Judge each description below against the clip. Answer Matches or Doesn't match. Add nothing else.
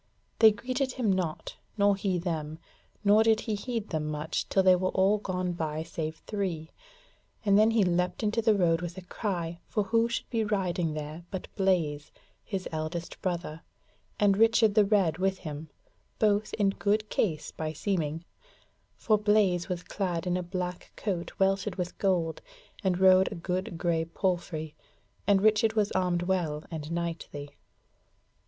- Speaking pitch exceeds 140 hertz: Matches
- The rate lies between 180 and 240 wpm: Doesn't match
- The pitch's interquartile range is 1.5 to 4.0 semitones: Matches